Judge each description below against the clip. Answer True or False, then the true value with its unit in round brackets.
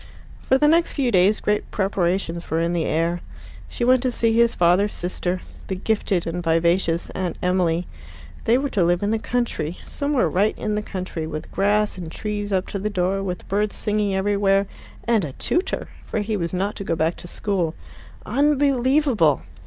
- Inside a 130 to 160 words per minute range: False (185 wpm)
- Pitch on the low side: False (195 Hz)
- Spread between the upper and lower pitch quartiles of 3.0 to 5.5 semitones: True (3.9 semitones)